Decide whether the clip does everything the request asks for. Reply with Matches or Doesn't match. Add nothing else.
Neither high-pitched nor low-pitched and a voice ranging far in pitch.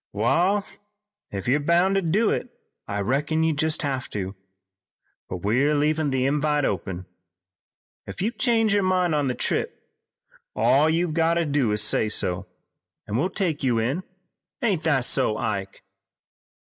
Matches